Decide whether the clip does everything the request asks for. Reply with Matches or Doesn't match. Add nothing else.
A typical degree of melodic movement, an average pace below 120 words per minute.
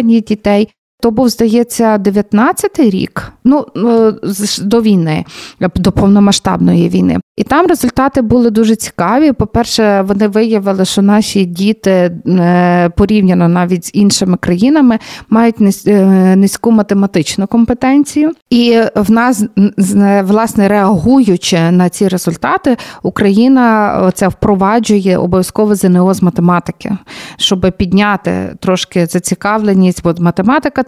Matches